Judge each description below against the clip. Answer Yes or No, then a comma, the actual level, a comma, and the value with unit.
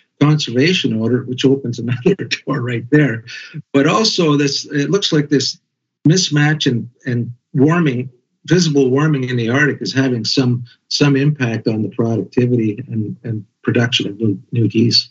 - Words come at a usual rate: Yes, average, 155 wpm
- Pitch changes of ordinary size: Yes, average, 3.6 semitones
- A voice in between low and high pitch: No, low, 130 Hz